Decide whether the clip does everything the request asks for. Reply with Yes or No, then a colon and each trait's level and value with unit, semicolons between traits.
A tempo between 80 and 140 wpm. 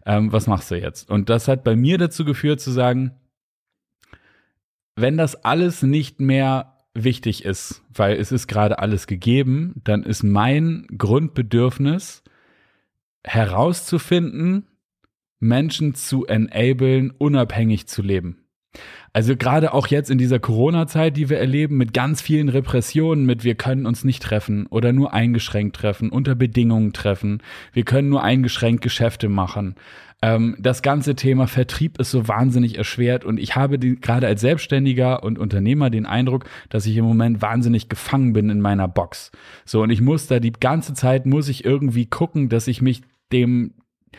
No: average, 160 wpm